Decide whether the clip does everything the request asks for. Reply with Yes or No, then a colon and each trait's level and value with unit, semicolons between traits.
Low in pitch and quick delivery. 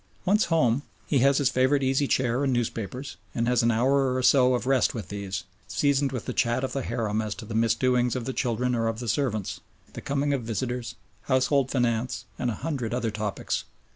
Yes: low, 125 Hz; fast, 210 wpm